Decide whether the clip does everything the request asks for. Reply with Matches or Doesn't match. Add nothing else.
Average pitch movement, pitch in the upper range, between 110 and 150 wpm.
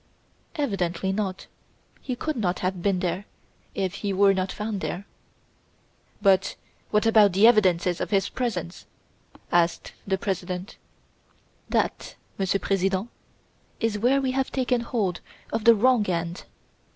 Matches